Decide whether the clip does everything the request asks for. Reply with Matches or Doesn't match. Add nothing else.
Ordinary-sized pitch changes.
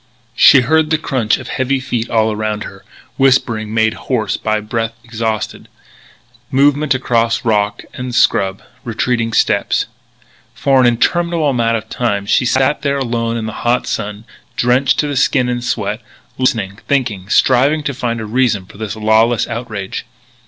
Matches